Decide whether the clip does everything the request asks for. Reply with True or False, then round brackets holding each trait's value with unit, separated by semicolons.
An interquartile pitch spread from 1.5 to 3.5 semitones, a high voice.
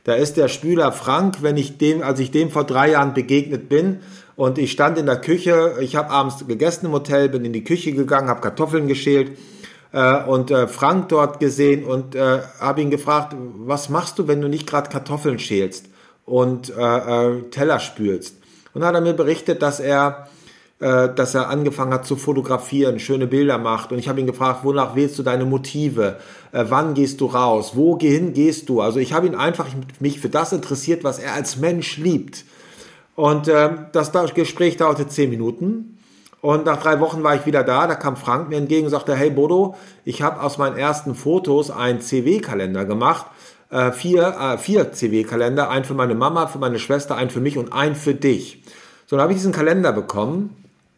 False (3.1 semitones; 140 Hz)